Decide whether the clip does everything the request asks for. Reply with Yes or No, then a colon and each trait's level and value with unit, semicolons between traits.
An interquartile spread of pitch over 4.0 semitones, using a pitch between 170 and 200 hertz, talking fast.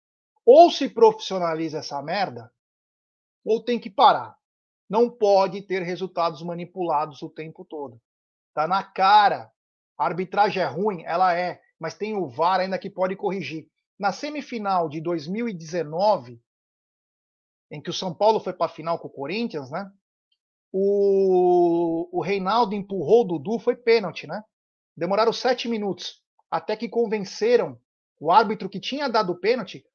No: average, 4.5 semitones; high, 190 Hz; average, 145 wpm